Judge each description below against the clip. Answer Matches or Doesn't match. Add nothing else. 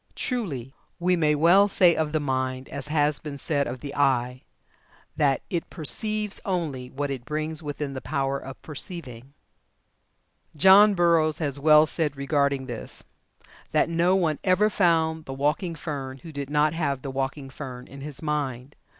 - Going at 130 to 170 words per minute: Matches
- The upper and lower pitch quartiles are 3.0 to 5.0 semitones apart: Matches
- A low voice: Doesn't match